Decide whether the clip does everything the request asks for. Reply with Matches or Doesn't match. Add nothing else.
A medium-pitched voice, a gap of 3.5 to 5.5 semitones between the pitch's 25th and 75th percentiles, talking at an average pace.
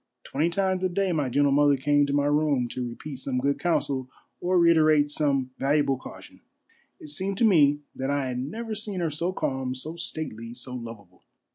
Matches